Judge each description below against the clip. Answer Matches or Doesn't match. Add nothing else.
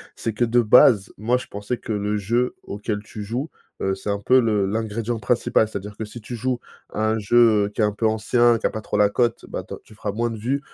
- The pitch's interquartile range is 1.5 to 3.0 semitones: Matches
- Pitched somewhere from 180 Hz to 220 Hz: Doesn't match